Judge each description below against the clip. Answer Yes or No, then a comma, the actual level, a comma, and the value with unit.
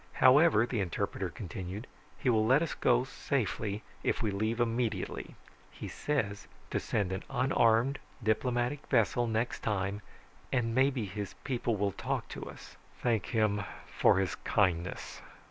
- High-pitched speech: No, low, 115 Hz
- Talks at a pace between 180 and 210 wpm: No, average, 145 wpm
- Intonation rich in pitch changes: No, average, 3.5 semitones